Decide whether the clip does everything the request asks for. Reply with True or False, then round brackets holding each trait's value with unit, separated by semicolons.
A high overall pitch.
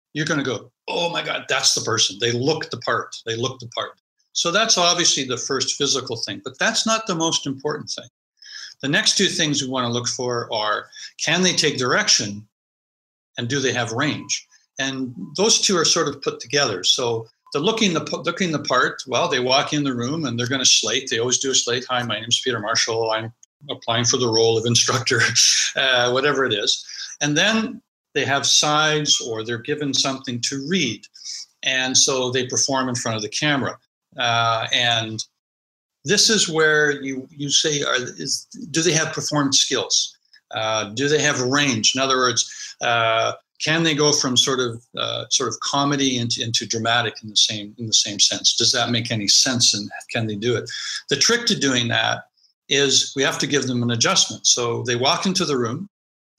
False (135 Hz)